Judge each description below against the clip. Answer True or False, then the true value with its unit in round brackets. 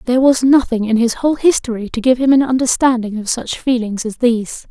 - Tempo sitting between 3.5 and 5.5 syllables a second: False (5.9 syllables/s)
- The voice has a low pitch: False (245 Hz)